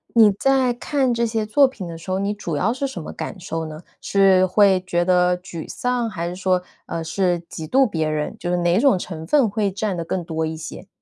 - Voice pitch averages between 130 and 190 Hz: Yes, medium, 185 Hz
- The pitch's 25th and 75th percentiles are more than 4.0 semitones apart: Yes, average, 4.5 semitones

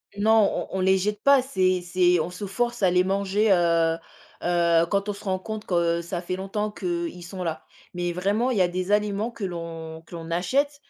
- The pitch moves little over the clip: No, average, 3.2 semitones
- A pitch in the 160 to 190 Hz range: Yes, medium, 185 Hz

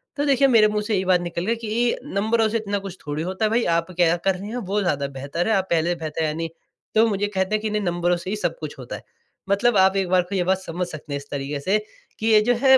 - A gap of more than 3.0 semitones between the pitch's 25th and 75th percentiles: Yes, average, 3.9 semitones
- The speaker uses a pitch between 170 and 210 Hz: Yes, high, 190 Hz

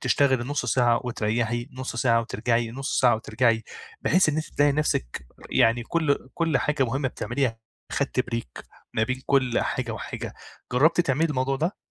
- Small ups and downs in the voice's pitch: No, average, 3.3 semitones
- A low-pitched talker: Yes, low, 130 Hz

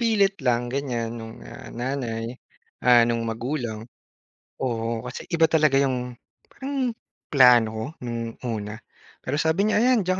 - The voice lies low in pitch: Yes, low, 125 Hz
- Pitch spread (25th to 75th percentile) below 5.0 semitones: No, wide, 5.6 semitones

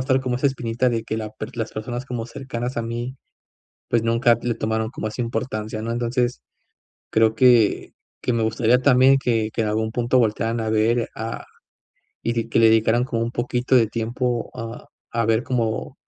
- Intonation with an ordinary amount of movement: No, narrow, 1.7 semitones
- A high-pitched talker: No, low, 115 Hz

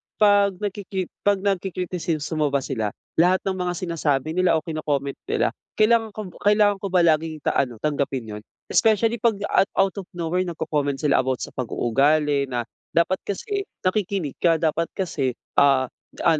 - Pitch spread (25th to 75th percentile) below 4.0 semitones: No, wide, 5.5 semitones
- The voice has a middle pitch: Yes, medium, 170 Hz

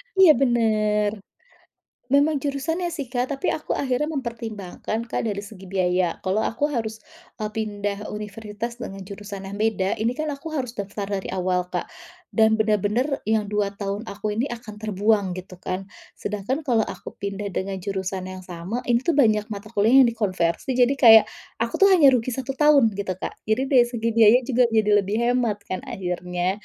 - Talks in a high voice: Yes, high, 215 Hz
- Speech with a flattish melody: No, average, 3.6 semitones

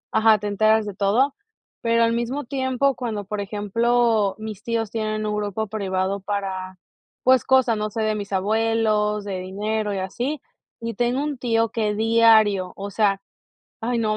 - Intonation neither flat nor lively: No, narrow, 2.2 semitones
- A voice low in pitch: No, high, 215 Hz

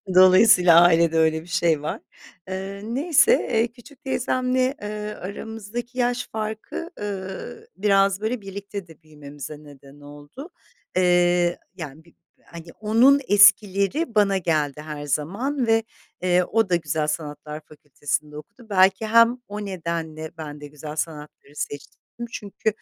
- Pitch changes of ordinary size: No, wide, 5.8 semitones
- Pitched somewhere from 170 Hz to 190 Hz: Yes, medium, 185 Hz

